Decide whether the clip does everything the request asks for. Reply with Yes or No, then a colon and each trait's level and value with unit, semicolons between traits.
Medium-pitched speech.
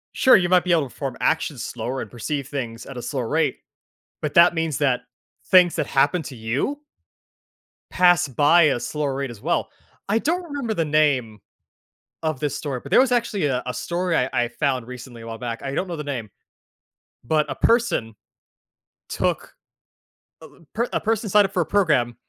Yes: medium, 150 Hz